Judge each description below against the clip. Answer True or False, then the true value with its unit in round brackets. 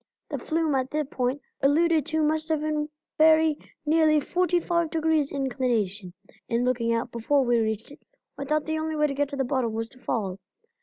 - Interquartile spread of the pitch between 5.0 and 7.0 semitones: False (4.3 semitones)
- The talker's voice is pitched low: False (285 Hz)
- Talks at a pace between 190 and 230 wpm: True (200 wpm)